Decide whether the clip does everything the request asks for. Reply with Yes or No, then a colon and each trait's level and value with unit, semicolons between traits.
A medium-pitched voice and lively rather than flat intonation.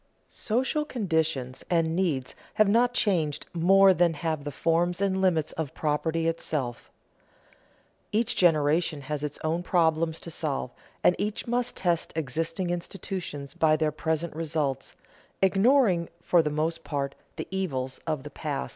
No: medium, 165 Hz; average, 3.7 semitones